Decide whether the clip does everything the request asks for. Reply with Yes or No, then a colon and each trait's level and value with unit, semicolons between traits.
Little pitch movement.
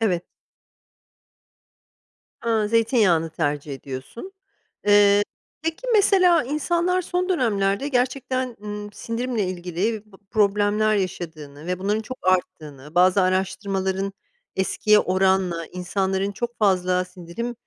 No: average, 4.3 semitones